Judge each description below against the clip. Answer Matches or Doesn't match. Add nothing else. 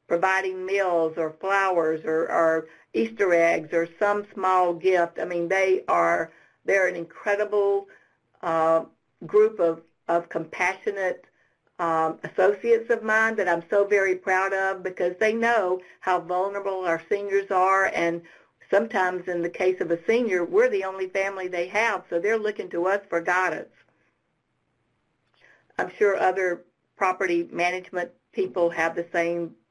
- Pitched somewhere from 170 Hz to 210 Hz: Matches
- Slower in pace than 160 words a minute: Matches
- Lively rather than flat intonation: Doesn't match